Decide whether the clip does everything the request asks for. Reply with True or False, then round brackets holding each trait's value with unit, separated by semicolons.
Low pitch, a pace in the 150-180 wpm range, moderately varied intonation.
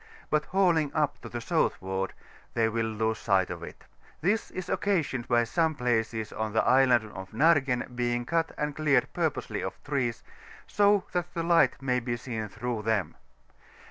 False (125 Hz; 170 wpm; 5.9 semitones)